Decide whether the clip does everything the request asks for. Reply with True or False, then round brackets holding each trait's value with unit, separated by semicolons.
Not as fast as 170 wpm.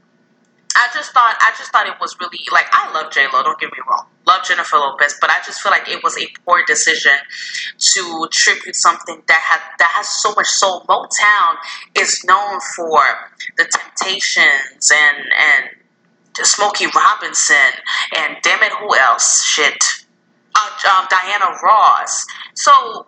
True (160 wpm)